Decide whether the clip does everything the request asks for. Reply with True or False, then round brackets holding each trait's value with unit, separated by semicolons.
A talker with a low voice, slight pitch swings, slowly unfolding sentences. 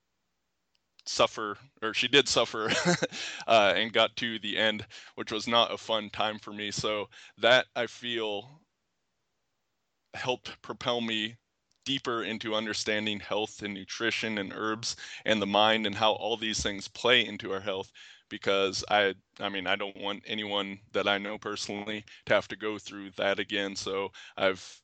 False (105 Hz; 1.6 semitones; 160 wpm)